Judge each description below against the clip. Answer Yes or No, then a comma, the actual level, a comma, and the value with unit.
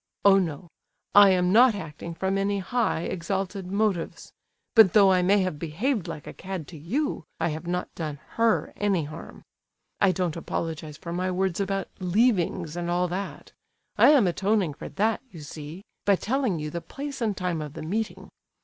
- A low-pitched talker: No, medium, 185 Hz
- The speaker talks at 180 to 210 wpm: Yes, average, 185 wpm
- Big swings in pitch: No, average, 3.4 semitones